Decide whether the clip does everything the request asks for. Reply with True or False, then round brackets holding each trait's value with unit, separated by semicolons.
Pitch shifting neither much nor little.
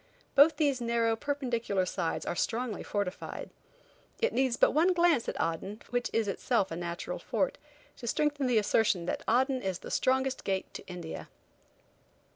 False (5.7 semitones)